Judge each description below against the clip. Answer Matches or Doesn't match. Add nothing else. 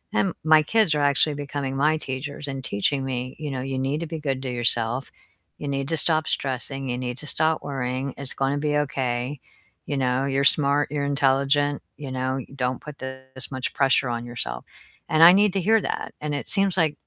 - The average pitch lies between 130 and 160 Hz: Matches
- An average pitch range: Doesn't match